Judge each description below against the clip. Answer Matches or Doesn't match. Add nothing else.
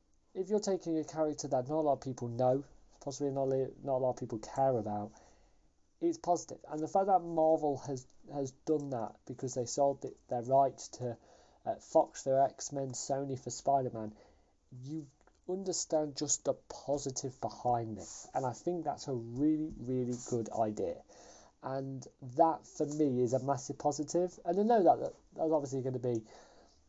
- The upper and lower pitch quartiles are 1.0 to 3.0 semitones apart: Doesn't match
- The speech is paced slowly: Doesn't match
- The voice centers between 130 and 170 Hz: Matches